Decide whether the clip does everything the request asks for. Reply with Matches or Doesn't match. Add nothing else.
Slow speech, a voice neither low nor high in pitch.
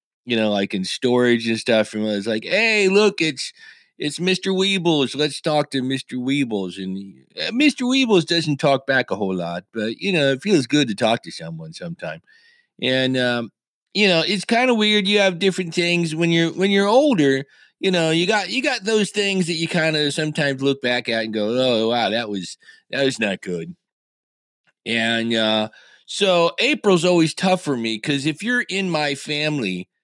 Doesn't match